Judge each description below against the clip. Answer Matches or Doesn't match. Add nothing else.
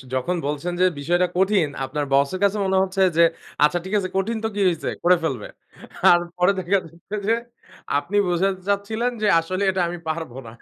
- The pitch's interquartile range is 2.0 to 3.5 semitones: Matches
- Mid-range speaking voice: Matches